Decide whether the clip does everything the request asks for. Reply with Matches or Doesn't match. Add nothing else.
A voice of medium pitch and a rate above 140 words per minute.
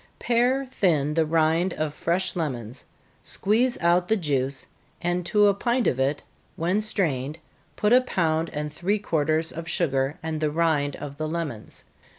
Matches